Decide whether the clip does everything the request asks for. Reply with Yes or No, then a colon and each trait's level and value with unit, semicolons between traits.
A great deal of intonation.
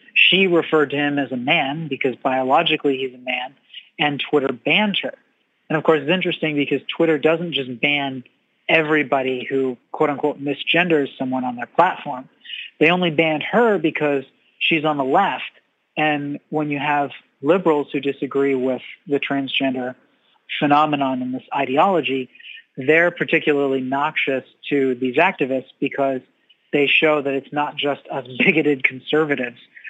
No: average, 2.7 semitones